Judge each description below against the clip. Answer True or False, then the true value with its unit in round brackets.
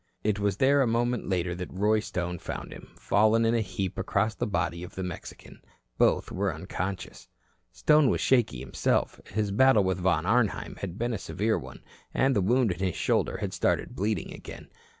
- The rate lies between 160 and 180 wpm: False (190 wpm)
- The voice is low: True (100 Hz)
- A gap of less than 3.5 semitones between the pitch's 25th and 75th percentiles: False (4.0 semitones)